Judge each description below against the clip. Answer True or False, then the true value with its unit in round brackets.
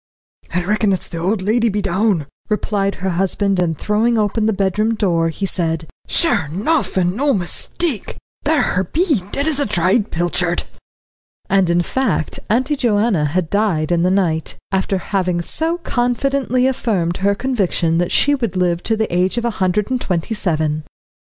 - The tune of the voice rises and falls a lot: False (4.9 semitones)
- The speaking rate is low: False (175 wpm)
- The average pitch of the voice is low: False (195 Hz)